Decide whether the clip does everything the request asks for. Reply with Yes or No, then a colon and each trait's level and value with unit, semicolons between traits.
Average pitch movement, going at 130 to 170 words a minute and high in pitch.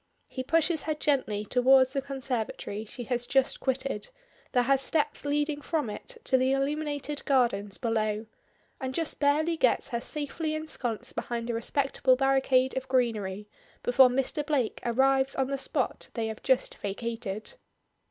Yes: average, 3.3 semitones; average, 150 wpm; very high, 260 Hz